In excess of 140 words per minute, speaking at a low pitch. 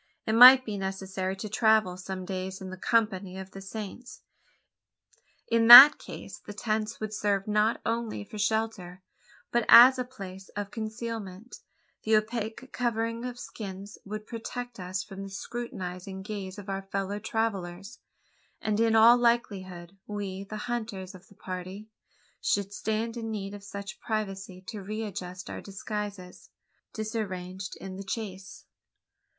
No: average, 150 wpm; high, 205 Hz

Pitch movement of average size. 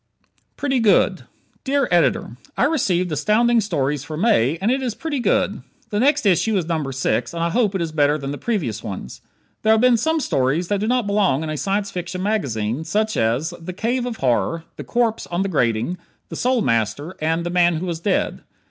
No: wide, 6.6 semitones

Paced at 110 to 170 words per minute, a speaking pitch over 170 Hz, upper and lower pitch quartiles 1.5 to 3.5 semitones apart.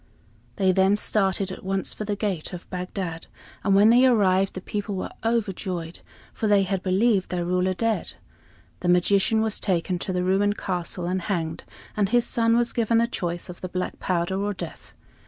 No: average, 190 wpm; high, 190 Hz; narrow, 2.6 semitones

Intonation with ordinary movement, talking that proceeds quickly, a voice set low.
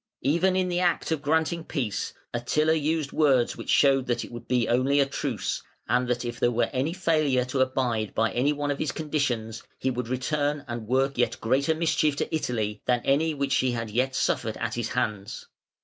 Yes: average, 4.0 semitones; fast, 210 wpm; low, 130 Hz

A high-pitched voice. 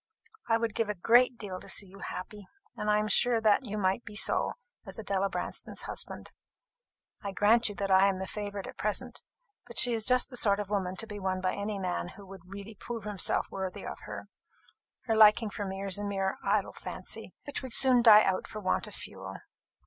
Yes: high, 205 Hz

